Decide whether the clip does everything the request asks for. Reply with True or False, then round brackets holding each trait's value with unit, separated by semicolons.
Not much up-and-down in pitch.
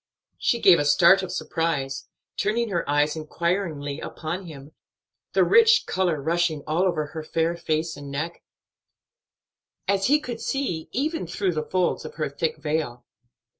False (3.8 semitones)